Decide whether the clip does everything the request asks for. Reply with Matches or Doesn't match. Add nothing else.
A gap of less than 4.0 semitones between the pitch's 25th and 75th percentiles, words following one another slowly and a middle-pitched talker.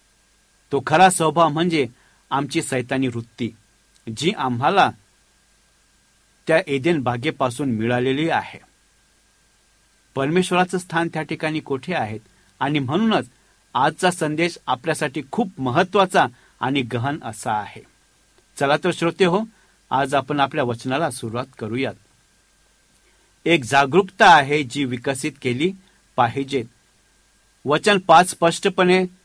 Doesn't match